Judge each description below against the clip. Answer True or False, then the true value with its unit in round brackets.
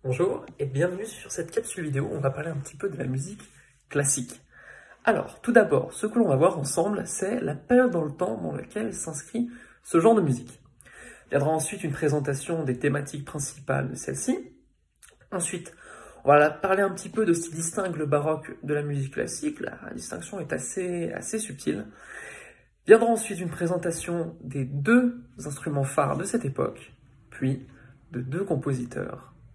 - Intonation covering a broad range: True (5.7 semitones)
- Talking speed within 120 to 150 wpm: False (175 wpm)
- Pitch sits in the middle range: True (160 Hz)